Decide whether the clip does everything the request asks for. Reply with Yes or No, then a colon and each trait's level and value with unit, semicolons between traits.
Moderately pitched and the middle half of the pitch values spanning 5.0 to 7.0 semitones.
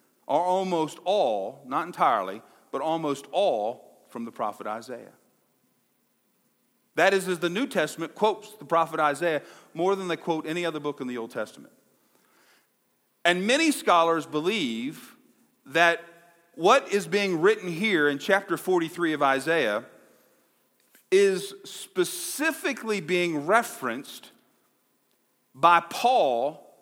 Yes: medium, 175 Hz; wide, 5.5 semitones